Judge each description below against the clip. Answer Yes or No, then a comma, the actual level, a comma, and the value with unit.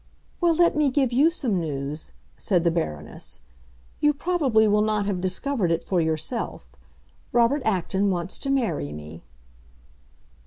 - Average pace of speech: Yes, average, 145 wpm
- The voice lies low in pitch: No, high, 205 Hz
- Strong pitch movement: Yes, wide, 8.6 semitones